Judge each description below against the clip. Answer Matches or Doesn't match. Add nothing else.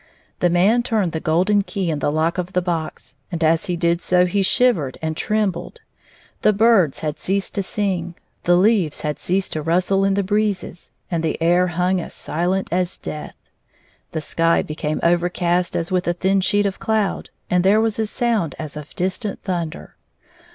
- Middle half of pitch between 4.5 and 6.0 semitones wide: Doesn't match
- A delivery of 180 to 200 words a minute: Matches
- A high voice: Doesn't match